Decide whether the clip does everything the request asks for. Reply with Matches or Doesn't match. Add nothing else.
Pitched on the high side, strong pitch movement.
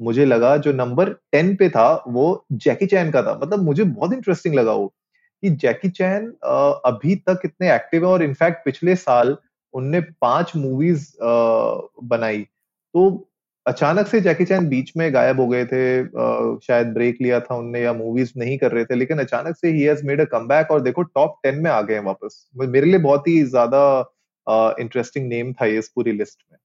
Doesn't match